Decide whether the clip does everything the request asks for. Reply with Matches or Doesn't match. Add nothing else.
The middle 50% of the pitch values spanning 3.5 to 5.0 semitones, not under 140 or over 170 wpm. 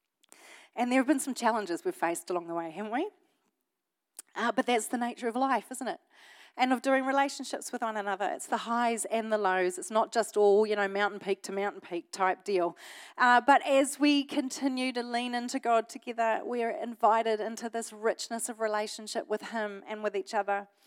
Doesn't match